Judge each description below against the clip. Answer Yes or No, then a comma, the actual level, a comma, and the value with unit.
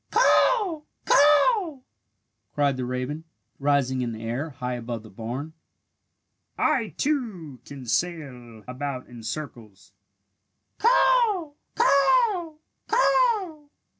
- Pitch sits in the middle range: Yes, medium, 150 Hz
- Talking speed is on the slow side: Yes, slow, 100 wpm